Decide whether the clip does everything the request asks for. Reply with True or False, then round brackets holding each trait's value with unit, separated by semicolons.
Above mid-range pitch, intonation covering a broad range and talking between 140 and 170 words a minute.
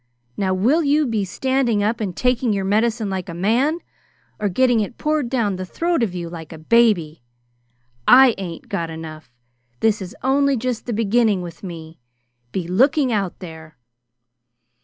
True (210 Hz; 5.9 semitones; 165 wpm)